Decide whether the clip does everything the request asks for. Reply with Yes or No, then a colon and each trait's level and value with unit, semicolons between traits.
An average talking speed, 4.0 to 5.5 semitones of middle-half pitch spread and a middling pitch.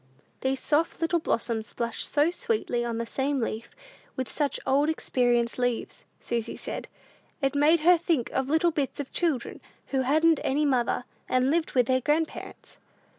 No: average, 165 wpm; average, 4.4 semitones; very high, 270 Hz